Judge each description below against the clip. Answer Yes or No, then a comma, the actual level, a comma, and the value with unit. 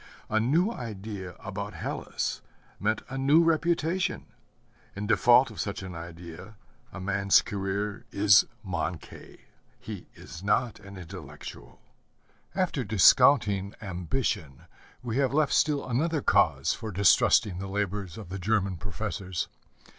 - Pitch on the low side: Yes, low, 105 Hz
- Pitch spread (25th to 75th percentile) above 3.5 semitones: Yes, average, 4.8 semitones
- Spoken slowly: Yes, slow, 125 wpm